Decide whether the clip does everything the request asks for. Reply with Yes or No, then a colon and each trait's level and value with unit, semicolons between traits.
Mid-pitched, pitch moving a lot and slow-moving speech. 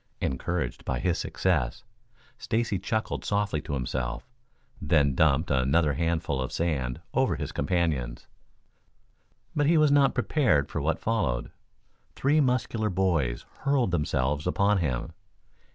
No: very low, 85 Hz; wide, 7.5 semitones; slow, 125 wpm